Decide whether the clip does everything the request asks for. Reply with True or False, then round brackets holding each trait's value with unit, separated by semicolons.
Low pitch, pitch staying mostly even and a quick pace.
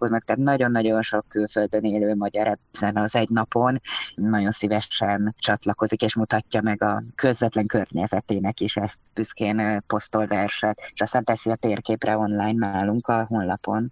False (110 Hz; 1.3 semitones; 140 wpm)